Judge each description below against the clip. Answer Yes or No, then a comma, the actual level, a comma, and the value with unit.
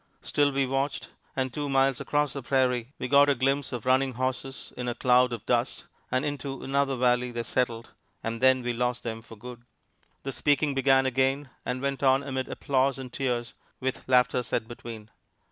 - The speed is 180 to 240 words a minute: Yes, average, 190 wpm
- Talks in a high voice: No, low, 130 Hz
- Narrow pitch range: Yes, narrow, 1.8 semitones